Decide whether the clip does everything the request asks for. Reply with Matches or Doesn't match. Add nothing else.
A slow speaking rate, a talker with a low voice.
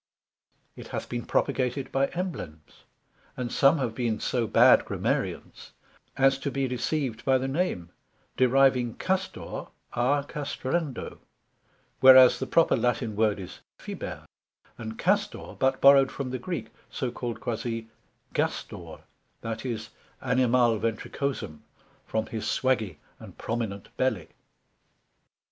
Matches